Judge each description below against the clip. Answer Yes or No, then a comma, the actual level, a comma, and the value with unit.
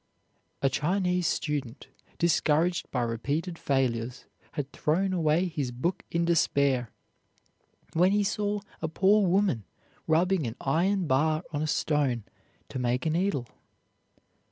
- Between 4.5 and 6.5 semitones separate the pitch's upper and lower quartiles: Yes, average, 5.1 semitones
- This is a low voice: No, medium, 155 Hz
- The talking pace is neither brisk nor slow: No, slow, 130 wpm